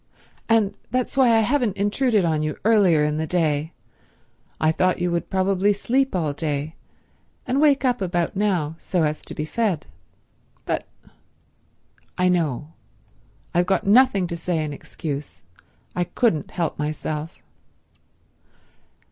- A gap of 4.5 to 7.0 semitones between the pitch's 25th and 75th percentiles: Yes, average, 5.2 semitones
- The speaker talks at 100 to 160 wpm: Yes, average, 140 wpm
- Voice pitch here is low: No, medium, 180 Hz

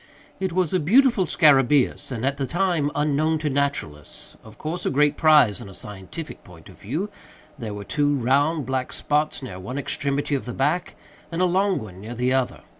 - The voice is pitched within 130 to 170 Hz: Yes, medium, 140 Hz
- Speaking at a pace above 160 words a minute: Yes, average, 190 wpm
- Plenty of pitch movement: No, average, 4.4 semitones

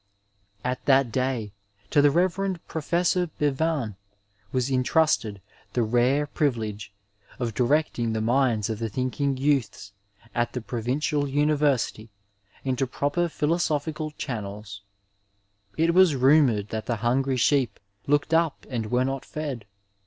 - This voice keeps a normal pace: No, slow, 130 wpm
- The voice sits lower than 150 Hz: Yes, low, 135 Hz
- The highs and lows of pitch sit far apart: No, average, 4.2 semitones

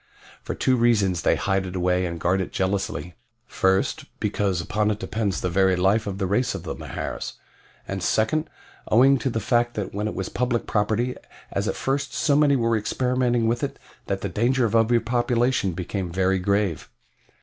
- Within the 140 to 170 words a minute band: No, average, 185 wpm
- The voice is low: Yes, low, 105 Hz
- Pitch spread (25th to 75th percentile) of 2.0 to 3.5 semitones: No, average, 4.0 semitones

